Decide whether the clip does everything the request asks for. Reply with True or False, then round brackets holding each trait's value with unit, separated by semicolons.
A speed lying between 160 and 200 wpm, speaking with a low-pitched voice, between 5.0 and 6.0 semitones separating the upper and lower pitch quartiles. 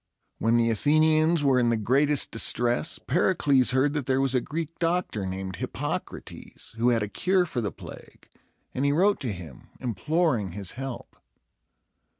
True (170 wpm; 130 Hz; 5.4 semitones)